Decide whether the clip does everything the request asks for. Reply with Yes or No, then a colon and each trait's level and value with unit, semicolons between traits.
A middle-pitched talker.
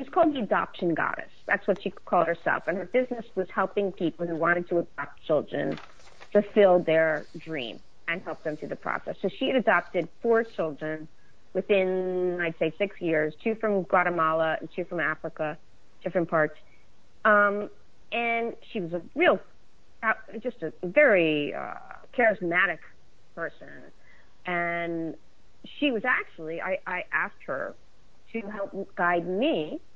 Yes: medium, 180 Hz